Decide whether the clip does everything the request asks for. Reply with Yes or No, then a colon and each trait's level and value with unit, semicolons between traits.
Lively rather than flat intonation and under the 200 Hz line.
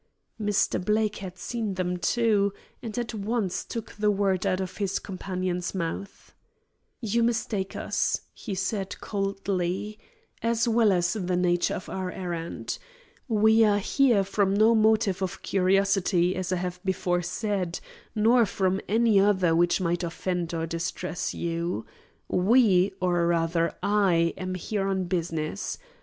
No: average, 2.9 semitones; high, 190 Hz